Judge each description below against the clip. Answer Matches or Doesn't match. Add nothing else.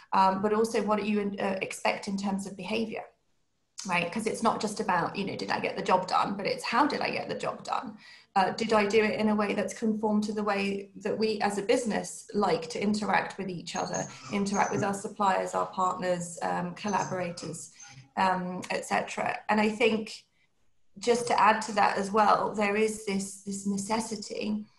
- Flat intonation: Matches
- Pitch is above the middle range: Matches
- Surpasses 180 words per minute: Matches